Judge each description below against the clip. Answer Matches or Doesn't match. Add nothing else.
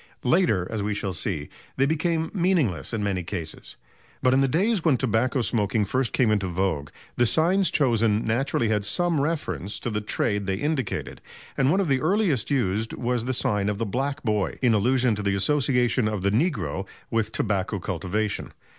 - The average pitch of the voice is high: Doesn't match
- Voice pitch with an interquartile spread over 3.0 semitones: Matches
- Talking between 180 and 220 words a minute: Matches